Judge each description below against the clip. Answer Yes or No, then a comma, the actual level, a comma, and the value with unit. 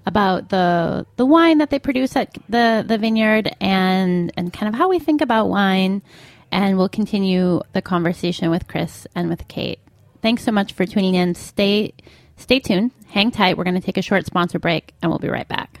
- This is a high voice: Yes, high, 195 Hz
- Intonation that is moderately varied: Yes, average, 3.7 semitones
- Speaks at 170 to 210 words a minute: Yes, fast, 205 wpm